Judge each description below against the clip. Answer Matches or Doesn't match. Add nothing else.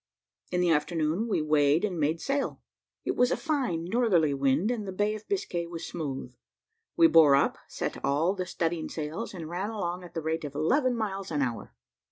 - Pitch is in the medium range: Matches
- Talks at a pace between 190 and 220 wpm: Matches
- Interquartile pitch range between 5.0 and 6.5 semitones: Matches